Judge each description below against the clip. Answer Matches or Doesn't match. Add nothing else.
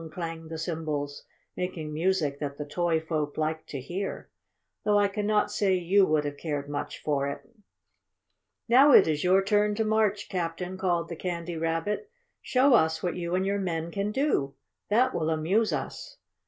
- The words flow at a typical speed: Matches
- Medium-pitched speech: Matches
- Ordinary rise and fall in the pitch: Matches